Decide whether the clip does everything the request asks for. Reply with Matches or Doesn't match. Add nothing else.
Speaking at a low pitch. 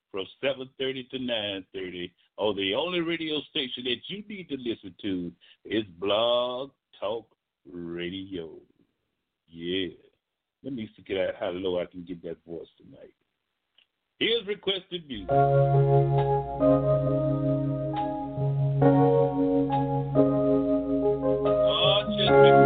Matches